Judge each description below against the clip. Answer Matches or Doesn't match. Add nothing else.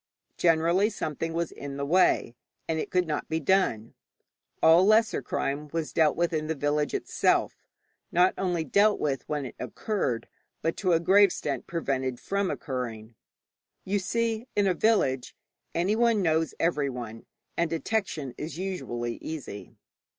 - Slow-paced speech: Doesn't match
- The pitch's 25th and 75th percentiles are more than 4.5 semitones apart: Matches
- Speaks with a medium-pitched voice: Matches